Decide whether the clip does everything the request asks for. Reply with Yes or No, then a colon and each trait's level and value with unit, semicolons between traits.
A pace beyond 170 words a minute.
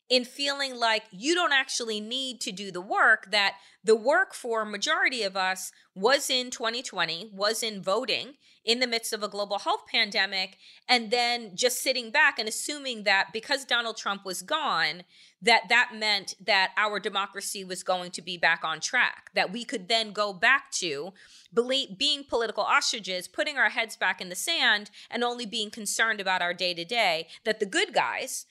Yes: average, 185 wpm